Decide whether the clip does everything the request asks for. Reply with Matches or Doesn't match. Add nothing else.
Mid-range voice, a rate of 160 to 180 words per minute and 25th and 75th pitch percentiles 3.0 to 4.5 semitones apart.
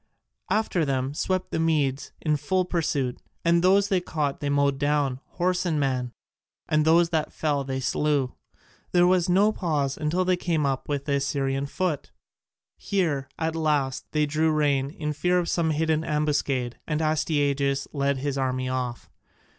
Matches